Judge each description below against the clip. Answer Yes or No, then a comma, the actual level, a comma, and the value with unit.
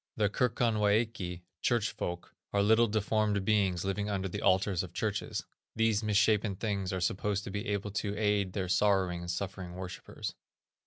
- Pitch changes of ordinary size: No, narrow, 2.2 semitones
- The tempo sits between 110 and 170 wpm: Yes, average, 160 wpm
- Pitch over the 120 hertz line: No, low, 100 Hz